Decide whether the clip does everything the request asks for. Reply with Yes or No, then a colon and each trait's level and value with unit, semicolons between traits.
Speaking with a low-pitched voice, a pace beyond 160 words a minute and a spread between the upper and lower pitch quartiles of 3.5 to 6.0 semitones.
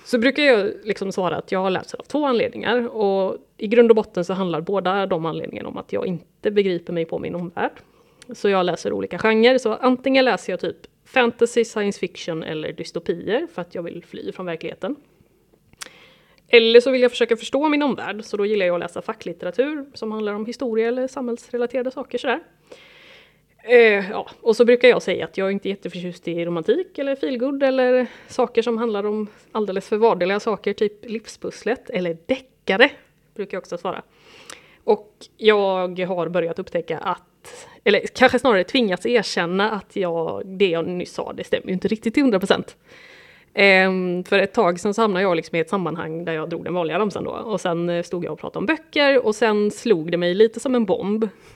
No: high, 215 Hz; average, 190 wpm; average, 5.2 semitones